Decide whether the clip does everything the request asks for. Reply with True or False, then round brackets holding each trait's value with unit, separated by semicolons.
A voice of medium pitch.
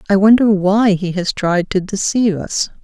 False (195 Hz)